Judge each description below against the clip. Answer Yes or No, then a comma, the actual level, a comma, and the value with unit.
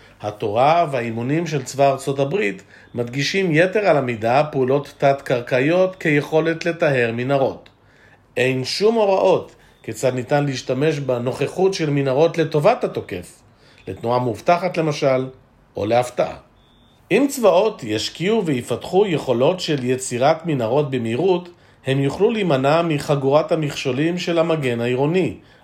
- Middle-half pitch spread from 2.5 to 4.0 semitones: No, average, 4.4 semitones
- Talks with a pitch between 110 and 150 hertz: Yes, medium, 140 Hz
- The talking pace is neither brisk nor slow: Yes, average, 110 wpm